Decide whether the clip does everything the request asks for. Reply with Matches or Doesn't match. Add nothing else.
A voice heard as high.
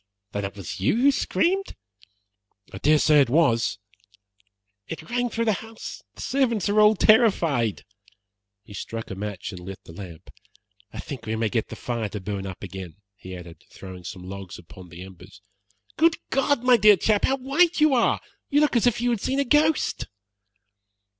Doesn't match